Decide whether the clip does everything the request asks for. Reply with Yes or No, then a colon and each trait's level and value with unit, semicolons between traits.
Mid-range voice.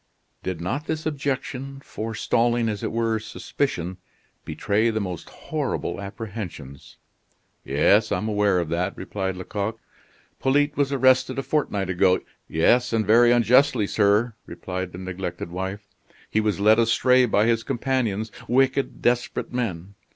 No: low, 110 Hz